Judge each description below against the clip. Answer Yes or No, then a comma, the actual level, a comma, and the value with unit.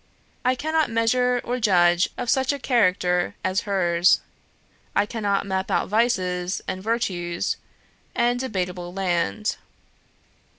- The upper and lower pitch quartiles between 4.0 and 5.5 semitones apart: Yes, average, 5.1 semitones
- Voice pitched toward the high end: Yes, high, 200 Hz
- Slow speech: Yes, slow, 120 wpm